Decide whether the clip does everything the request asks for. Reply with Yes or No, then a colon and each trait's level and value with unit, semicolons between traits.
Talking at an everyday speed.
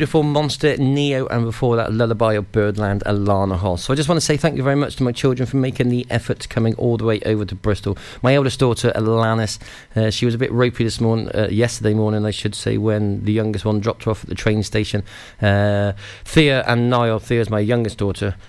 No: fast, 235 wpm